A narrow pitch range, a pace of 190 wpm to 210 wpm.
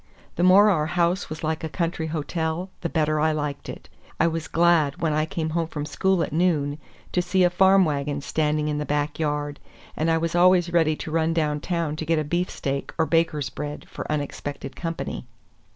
Yes: narrow, 2.3 semitones; average, 200 wpm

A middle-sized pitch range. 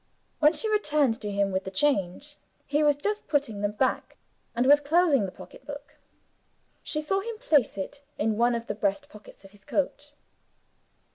No: wide, 6.3 semitones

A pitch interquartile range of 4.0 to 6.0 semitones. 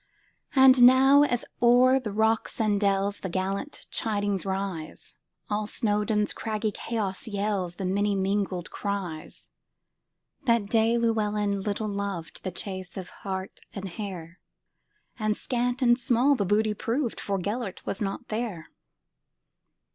No: average, 3.1 semitones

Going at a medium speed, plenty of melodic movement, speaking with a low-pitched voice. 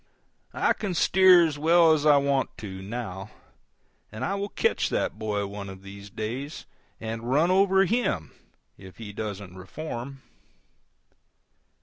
Yes: average, 145 wpm; wide, 8.4 semitones; low, 120 Hz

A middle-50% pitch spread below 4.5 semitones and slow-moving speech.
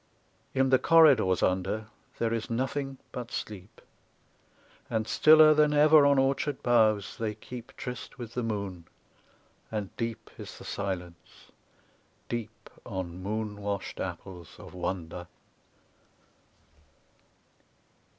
No: wide, 5.4 semitones; slow, 110 wpm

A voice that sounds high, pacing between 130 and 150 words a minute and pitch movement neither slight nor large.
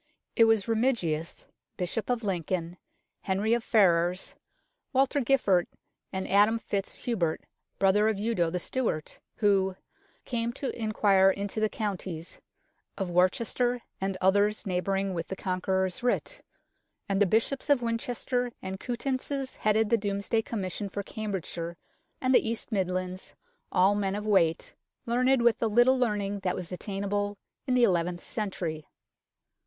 Yes: high, 205 Hz; average, 145 wpm; average, 3.7 semitones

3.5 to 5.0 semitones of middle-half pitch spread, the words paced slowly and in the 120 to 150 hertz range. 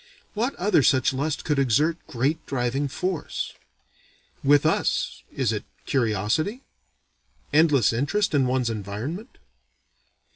Yes: average, 4.7 semitones; slow, 110 wpm; medium, 140 Hz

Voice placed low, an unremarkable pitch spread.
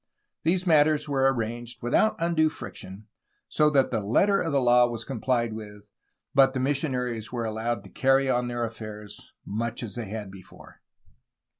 Yes: low, 120 Hz; average, 3.8 semitones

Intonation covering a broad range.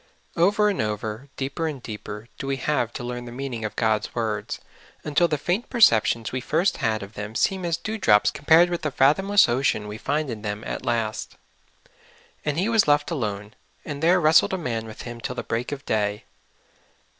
Yes: wide, 6.6 semitones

